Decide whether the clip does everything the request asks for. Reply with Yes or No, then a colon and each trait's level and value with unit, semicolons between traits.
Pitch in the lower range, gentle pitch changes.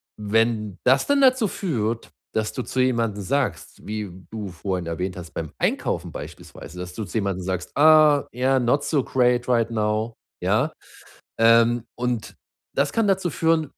No: low, 115 Hz; average, 5.0 semitones